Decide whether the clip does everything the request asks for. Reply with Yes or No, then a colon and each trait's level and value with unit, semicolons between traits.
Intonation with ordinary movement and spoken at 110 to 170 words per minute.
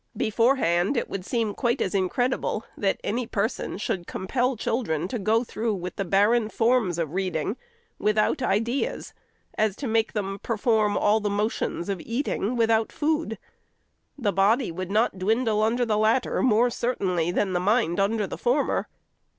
Yes: average, 3.3 semitones; average, 160 wpm